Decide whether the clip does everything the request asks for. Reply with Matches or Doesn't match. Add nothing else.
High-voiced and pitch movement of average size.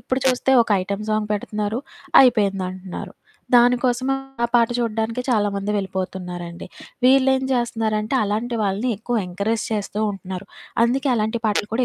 Matches